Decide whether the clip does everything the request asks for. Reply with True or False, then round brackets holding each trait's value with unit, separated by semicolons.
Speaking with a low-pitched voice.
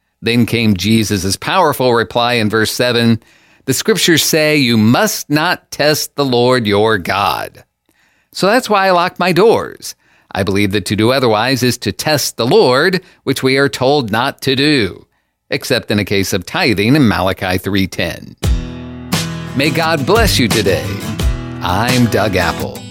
True (120 Hz)